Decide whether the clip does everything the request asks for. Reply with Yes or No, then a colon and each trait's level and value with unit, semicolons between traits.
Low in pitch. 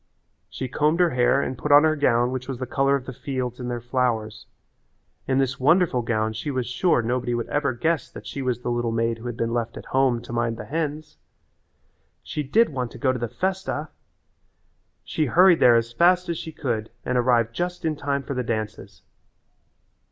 Yes: low, 130 Hz